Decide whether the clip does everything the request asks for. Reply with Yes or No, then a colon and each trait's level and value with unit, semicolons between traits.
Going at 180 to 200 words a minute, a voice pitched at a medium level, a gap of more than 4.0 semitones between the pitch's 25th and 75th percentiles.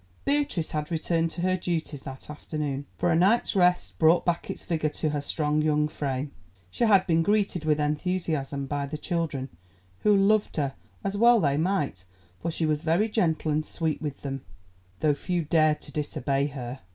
No: average, 185 wpm; medium, 155 Hz; average, 3.3 semitones